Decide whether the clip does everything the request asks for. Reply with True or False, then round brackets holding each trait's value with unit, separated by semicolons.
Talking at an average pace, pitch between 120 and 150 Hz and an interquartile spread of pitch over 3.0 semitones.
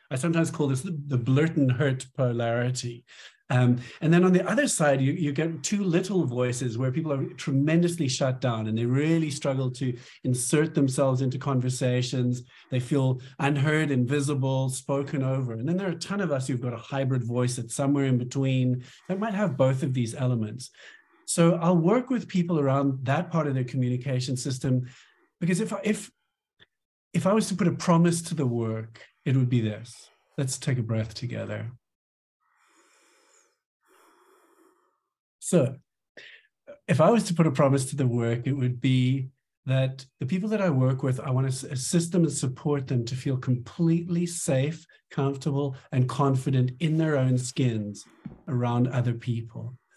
True (175 wpm; 135 Hz; 4.5 semitones)